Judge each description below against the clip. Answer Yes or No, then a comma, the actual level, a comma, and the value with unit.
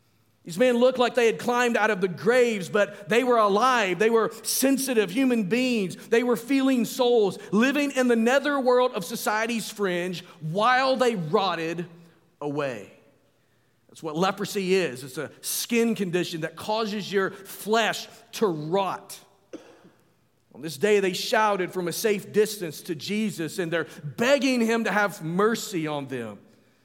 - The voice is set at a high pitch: Yes, high, 210 Hz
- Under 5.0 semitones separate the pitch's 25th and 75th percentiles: No, average, 5.3 semitones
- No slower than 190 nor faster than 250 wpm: No, average, 155 wpm